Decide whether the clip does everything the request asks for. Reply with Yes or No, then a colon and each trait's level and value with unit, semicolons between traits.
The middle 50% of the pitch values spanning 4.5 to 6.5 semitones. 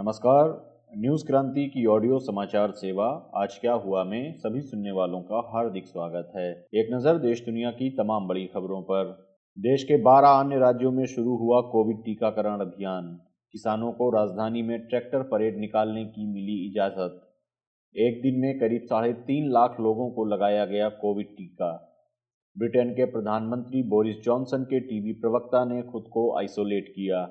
No: average, 3.2 semitones